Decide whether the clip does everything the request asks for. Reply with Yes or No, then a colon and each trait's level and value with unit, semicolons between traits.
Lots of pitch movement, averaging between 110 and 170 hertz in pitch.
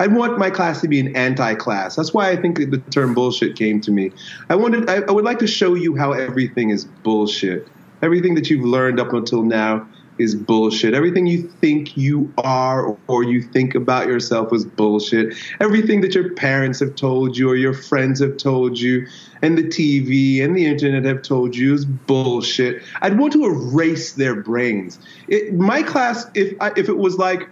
Yes: wide, 6.1 semitones; low, 135 Hz